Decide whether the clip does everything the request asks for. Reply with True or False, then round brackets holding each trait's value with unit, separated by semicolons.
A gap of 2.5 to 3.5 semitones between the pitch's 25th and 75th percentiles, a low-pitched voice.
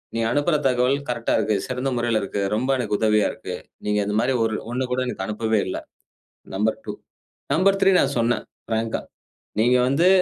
True (3.1 semitones; 120 Hz)